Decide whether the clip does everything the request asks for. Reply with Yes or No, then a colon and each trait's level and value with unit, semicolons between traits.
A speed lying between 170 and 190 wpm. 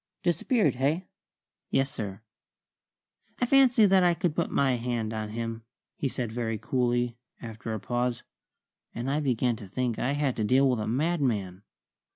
No: average, 160 wpm